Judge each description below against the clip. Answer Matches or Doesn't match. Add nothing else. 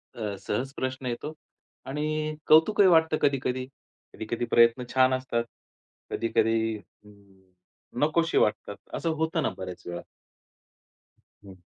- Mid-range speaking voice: Doesn't match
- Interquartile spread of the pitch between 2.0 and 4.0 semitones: Doesn't match